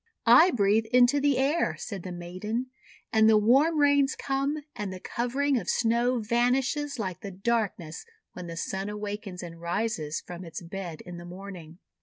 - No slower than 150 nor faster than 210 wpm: Yes, average, 170 wpm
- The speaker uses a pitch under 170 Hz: No, high, 215 Hz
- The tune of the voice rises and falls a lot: Yes, wide, 5.9 semitones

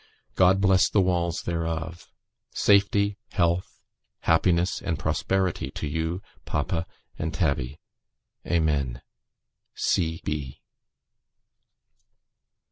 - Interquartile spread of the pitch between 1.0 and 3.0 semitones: Yes, narrow, 2.6 semitones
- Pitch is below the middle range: Yes, very low, 85 Hz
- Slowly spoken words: Yes, slow, 75 wpm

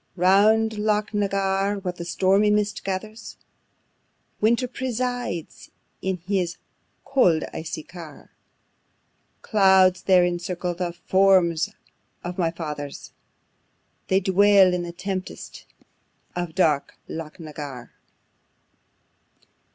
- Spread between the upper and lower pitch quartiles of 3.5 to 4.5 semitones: No, average, 2.9 semitones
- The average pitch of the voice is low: No, medium, 185 Hz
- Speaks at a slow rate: Yes, slow, 105 wpm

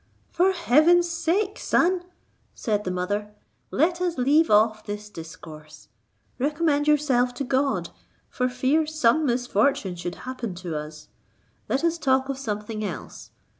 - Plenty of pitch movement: Yes, wide, 7.0 semitones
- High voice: Yes, very high, 255 Hz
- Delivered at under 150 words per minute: Yes, slow, 135 wpm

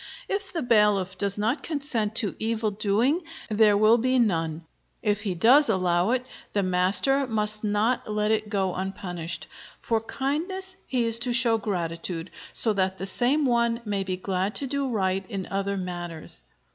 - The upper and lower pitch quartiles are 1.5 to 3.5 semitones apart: No, average, 4.1 semitones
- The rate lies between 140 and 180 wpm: Yes, average, 170 wpm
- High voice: Yes, high, 210 Hz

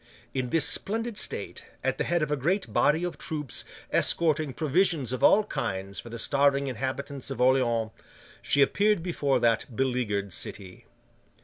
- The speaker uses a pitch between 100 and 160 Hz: Yes, medium, 140 Hz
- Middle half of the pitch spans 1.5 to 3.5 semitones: No, average, 5.1 semitones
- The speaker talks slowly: No, average, 155 wpm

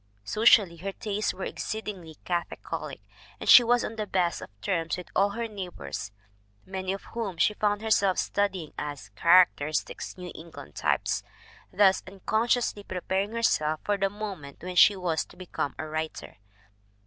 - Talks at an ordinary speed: Yes, average, 160 wpm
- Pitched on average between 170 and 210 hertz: Yes, high, 190 Hz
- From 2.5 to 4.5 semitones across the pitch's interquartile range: Yes, average, 3.6 semitones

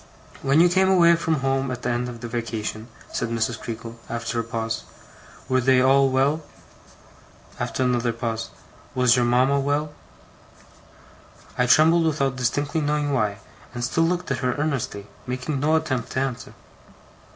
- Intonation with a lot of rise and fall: No, average, 3.6 semitones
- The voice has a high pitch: No, low, 130 Hz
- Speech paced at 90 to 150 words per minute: No, average, 160 wpm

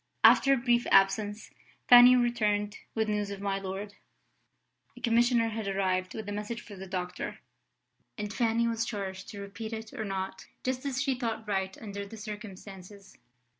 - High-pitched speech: Yes, high, 210 Hz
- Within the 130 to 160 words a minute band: No, average, 170 wpm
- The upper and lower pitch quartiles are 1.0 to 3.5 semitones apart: Yes, average, 2.8 semitones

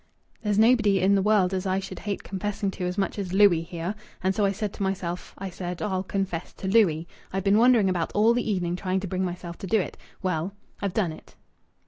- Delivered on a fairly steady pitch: Yes, narrow, 2.2 semitones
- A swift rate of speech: Yes, fast, 230 wpm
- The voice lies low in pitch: No, high, 190 Hz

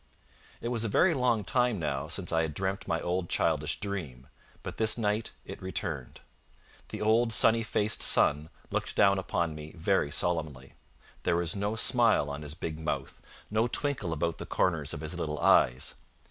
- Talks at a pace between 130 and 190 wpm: Yes, average, 175 wpm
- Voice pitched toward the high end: No, very low, 90 Hz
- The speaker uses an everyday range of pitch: No, wide, 5.9 semitones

